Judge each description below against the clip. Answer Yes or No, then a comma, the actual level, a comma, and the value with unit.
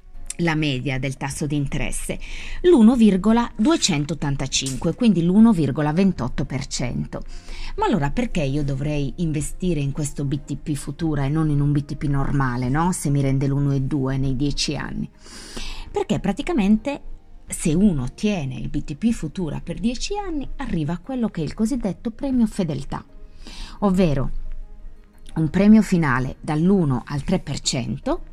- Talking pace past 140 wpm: No, average, 125 wpm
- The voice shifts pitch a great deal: Yes, wide, 6.4 semitones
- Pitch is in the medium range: Yes, medium, 155 Hz